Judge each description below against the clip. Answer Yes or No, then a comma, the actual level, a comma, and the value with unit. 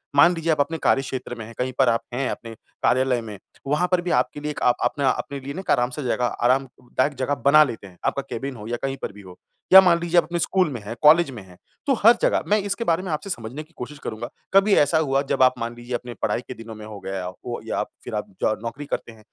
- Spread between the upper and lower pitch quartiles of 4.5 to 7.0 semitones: Yes, average, 4.8 semitones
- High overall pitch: No, low, 130 Hz